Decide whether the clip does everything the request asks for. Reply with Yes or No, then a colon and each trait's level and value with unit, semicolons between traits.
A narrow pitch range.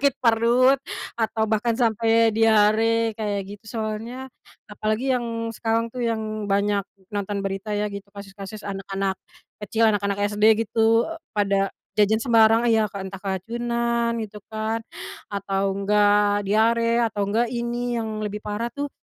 Yes: narrow, 2.1 semitones